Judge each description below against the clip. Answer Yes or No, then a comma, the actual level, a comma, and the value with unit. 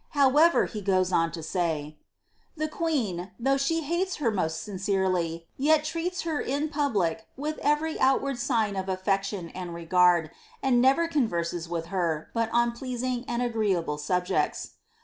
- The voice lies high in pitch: Yes, high, 220 Hz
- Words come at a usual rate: Yes, average, 160 wpm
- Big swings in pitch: Yes, wide, 7.7 semitones